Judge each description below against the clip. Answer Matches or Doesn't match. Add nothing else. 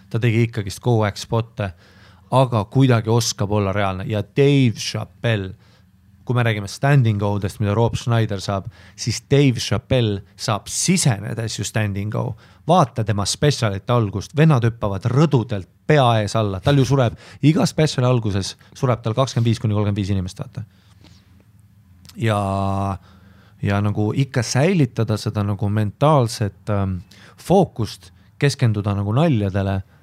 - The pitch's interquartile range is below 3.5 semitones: Doesn't match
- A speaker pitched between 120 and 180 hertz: Doesn't match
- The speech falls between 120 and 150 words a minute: Matches